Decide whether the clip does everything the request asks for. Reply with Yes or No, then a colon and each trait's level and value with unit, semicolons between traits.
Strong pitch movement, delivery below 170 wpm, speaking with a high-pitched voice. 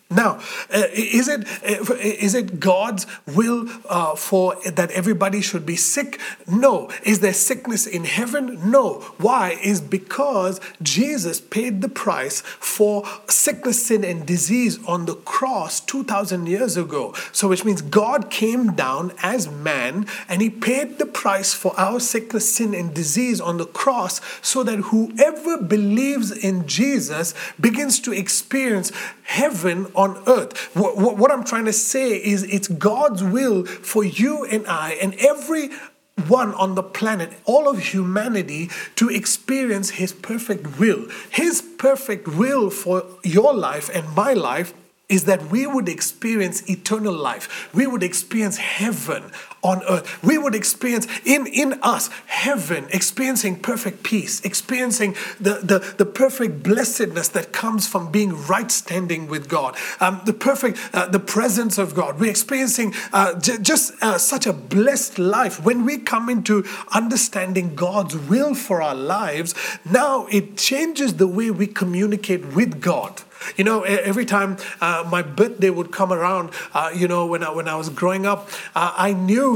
No: average, 4.3 semitones; average, 160 wpm; high, 205 Hz